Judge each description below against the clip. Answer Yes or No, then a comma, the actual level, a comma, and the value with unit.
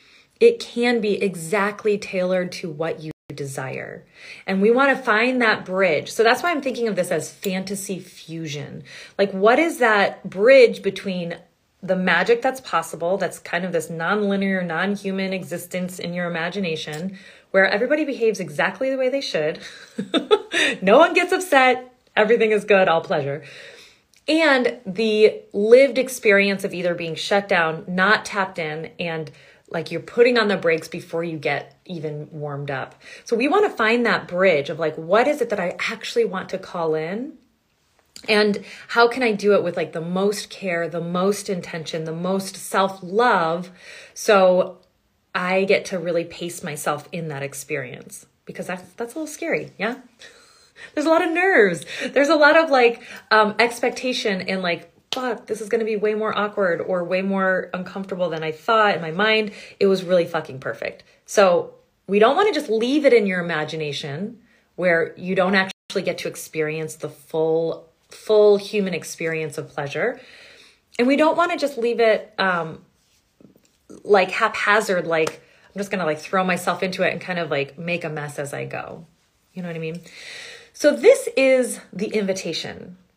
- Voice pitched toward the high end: Yes, high, 195 Hz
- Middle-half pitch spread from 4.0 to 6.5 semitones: Yes, wide, 5.6 semitones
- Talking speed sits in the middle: Yes, average, 180 wpm